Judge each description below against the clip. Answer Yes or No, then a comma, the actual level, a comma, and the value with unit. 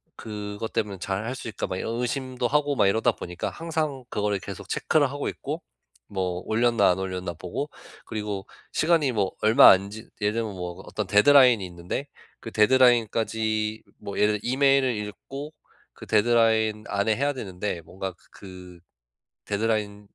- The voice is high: No, low, 110 Hz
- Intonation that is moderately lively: Yes, average, 4.0 semitones